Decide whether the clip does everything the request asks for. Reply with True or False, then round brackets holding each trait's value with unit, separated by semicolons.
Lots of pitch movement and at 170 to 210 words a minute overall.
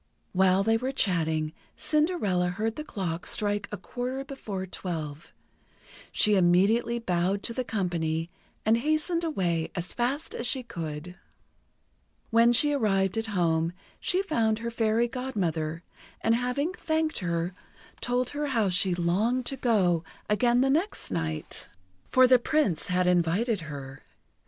False (6.2 semitones; 140 wpm)